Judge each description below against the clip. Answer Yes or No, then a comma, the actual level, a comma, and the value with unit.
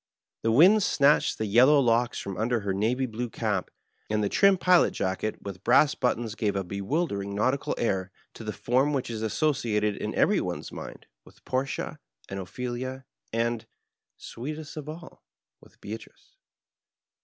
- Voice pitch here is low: Yes, low, 115 Hz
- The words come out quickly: No, average, 155 wpm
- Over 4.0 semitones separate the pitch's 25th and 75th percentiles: Yes, average, 4.6 semitones